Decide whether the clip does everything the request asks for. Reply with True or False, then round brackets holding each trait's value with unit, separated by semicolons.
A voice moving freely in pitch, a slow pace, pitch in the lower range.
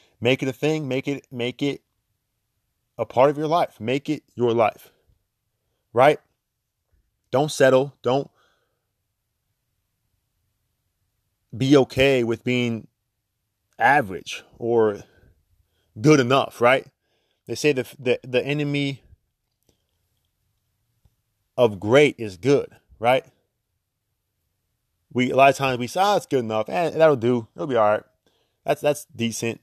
False (4.0 semitones; 125 wpm; 115 Hz)